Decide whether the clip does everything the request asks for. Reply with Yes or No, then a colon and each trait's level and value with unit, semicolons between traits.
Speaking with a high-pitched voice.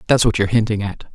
No: low, 105 Hz